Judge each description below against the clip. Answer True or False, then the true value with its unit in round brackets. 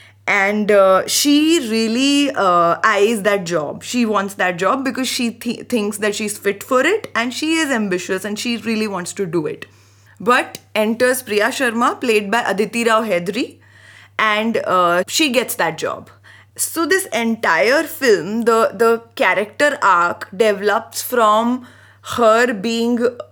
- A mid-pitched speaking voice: False (225 Hz)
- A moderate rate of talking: True (150 wpm)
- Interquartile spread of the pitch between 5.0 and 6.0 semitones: False (3.7 semitones)